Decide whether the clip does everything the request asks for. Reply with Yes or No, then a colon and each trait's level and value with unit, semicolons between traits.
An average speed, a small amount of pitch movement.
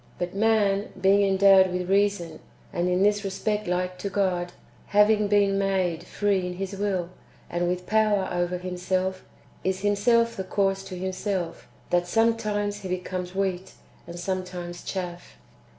Yes: average, 150 wpm; narrow, 2.1 semitones